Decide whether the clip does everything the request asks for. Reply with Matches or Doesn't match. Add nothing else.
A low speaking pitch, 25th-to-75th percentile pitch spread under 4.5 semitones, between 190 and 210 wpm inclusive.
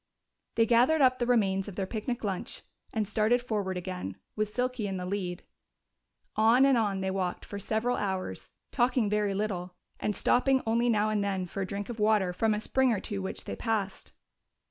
Doesn't match